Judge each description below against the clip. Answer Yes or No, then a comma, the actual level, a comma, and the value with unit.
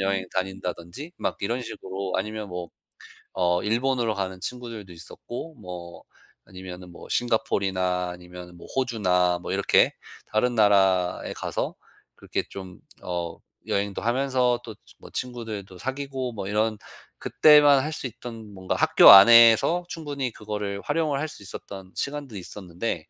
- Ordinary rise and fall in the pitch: Yes, average, 5.0 semitones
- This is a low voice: Yes, low, 105 Hz